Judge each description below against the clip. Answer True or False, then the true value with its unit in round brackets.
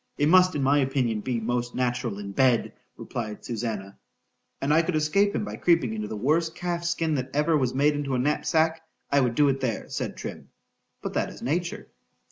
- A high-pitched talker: False (135 Hz)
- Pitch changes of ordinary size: True (4.8 semitones)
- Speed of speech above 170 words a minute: True (190 wpm)